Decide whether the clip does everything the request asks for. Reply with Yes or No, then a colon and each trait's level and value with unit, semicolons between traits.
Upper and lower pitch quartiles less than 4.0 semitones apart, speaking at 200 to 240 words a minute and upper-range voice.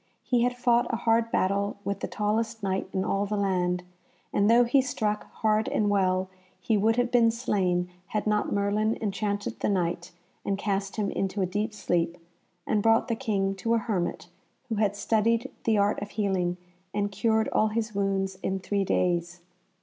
No: narrow, 2.6 semitones; average, 185 wpm; high, 205 Hz